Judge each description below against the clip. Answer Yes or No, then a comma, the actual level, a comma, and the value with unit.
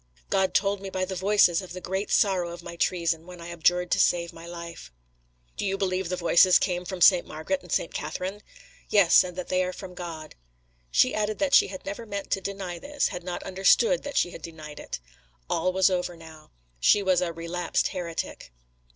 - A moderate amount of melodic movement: No, narrow, 2.1 semitones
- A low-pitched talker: No, medium, 180 Hz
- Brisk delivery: Yes, fast, 210 wpm